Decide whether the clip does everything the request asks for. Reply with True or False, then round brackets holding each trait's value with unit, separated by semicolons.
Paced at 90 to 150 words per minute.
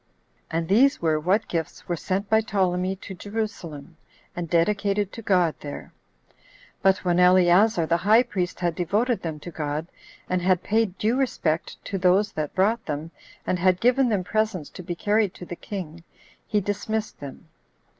False (175 wpm)